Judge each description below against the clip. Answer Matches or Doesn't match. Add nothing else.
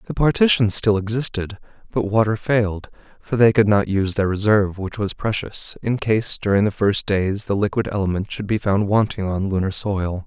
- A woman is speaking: Doesn't match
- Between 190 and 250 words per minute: Matches